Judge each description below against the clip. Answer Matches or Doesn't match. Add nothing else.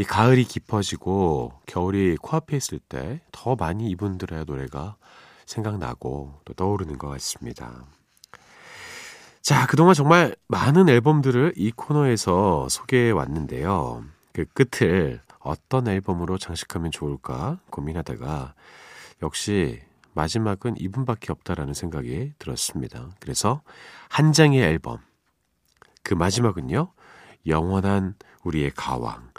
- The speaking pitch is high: Doesn't match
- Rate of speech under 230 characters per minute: Doesn't match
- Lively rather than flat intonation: Matches